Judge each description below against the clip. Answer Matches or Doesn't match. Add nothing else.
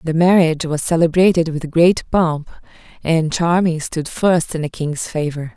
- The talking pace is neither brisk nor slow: Matches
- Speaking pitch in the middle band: Matches